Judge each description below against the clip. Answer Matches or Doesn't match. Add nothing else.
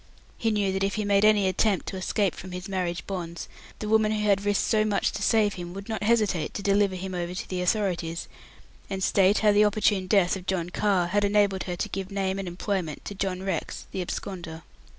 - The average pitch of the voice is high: Matches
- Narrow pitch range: Matches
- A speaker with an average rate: Doesn't match